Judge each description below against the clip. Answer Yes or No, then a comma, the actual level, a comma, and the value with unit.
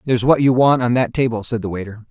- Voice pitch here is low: Yes, low, 120 Hz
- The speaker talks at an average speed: No, fast, 285 wpm